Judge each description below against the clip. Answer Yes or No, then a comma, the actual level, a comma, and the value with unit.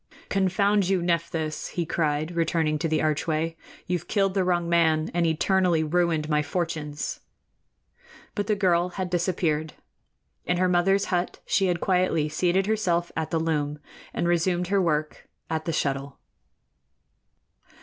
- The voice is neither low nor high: Yes, medium, 170 Hz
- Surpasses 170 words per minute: No, average, 145 wpm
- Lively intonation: No, narrow, 2.6 semitones